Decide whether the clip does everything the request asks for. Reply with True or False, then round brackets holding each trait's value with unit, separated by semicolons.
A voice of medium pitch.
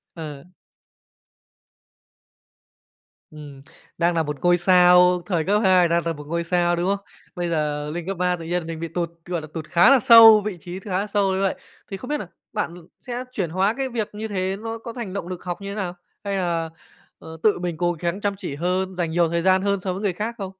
True (180 Hz)